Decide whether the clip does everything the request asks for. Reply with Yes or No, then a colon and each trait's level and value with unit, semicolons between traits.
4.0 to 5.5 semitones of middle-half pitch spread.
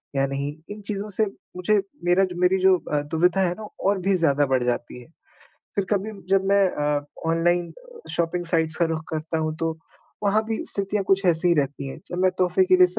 No: average, 3.6 semitones